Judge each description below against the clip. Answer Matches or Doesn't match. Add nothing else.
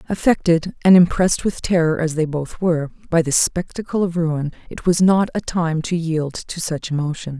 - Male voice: Doesn't match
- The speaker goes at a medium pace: Matches